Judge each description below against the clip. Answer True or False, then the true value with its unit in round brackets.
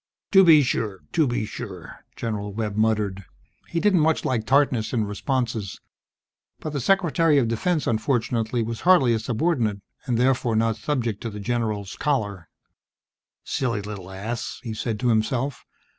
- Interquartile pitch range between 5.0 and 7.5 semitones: False (4.1 semitones)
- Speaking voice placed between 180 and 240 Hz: False (115 Hz)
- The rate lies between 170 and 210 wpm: False (155 wpm)